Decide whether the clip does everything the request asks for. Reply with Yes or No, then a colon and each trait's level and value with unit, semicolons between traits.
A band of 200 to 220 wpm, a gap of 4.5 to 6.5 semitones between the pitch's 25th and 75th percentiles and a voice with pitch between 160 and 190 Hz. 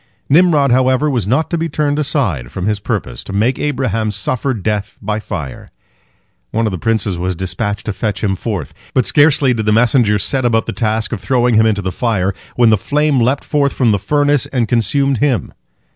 No: fast, 205 wpm; average, 4.9 semitones; low, 115 Hz